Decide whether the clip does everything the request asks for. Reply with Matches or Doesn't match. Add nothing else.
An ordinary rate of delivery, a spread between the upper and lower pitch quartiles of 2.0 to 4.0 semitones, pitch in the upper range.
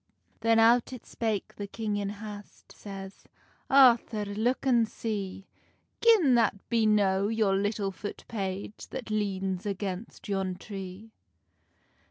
Doesn't match